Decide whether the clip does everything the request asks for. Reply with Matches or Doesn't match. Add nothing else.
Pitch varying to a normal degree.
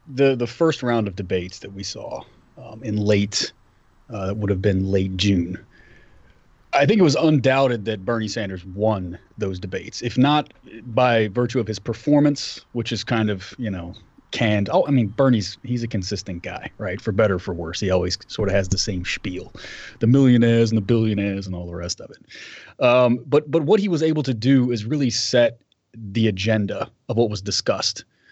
Matches